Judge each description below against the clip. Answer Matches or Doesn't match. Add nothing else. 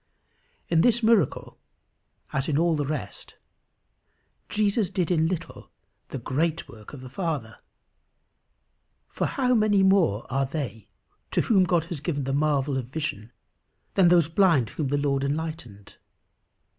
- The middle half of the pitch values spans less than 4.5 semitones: Doesn't match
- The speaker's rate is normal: Matches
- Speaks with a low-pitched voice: Doesn't match